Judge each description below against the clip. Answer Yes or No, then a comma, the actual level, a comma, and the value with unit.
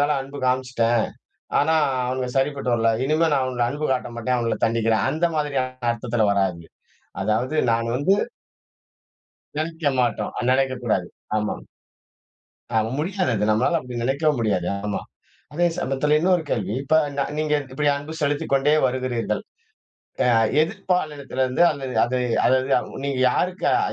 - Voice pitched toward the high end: No, low, 130 Hz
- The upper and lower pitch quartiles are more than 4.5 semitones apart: No, average, 3.8 semitones